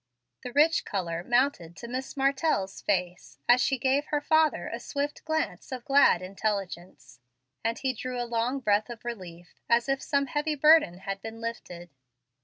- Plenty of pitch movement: Yes, wide, 6.2 semitones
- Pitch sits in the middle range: No, high, 240 Hz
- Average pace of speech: Yes, average, 170 wpm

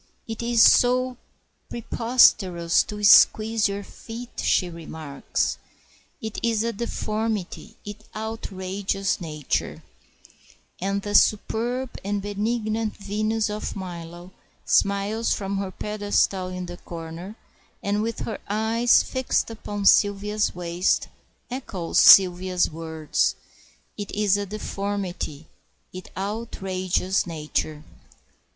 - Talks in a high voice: Yes, high, 200 Hz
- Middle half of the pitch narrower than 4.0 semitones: Yes, average, 3.2 semitones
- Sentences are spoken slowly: Yes, slow, 105 wpm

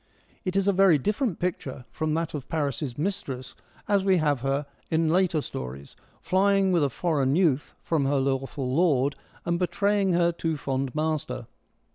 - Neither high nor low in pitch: Yes, medium, 155 Hz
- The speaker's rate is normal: Yes, average, 165 wpm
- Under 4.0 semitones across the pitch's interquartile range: No, average, 5.0 semitones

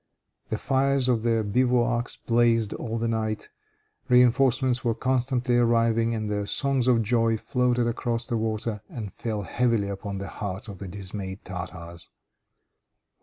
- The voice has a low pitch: Yes, low, 115 Hz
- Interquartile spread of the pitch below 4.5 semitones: Yes, average, 2.8 semitones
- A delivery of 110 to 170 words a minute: Yes, average, 145 wpm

